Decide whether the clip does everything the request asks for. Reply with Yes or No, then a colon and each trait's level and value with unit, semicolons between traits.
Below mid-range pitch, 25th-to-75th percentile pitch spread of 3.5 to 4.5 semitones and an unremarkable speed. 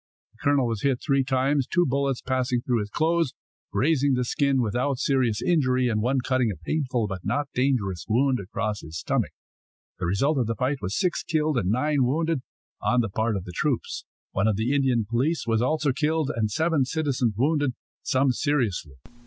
Yes: low, 130 Hz; average, 4.1 semitones; average, 190 wpm